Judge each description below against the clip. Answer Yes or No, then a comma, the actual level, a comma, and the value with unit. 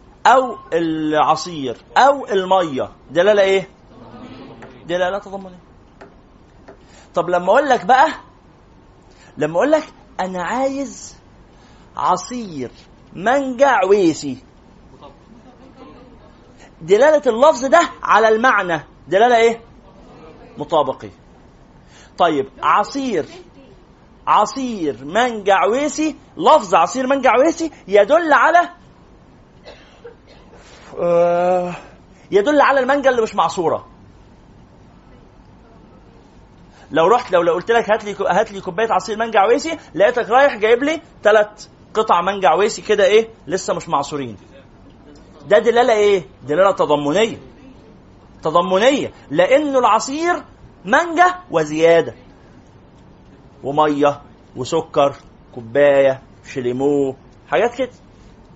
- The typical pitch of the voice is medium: No, high, 205 Hz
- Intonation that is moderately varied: No, wide, 8.5 semitones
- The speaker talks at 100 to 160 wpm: No, average, 90 wpm